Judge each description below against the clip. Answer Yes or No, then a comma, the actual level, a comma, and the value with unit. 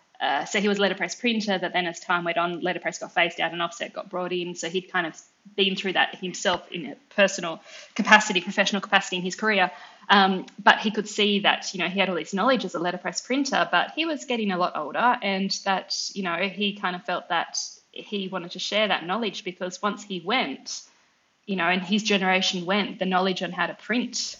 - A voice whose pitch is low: No, high, 190 Hz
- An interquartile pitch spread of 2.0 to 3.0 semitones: Yes, narrow, 2.6 semitones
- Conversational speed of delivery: No, fast, 230 wpm